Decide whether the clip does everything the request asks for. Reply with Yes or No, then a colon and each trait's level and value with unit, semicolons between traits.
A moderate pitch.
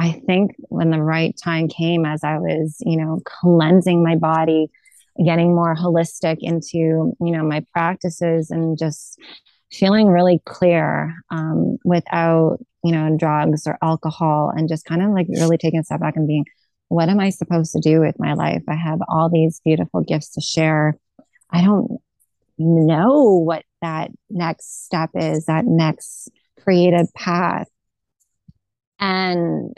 Yes: medium, 165 Hz